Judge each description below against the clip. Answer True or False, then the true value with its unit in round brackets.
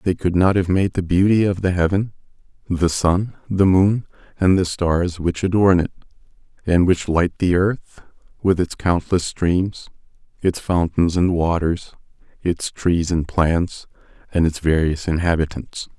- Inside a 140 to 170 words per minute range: True (155 wpm)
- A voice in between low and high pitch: False (90 Hz)